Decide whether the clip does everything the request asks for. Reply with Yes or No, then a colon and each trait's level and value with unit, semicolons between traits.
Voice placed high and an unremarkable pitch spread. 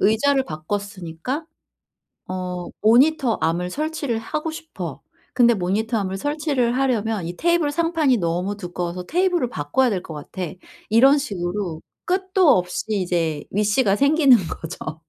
No: high, 220 Hz; wide, 8.1 semitones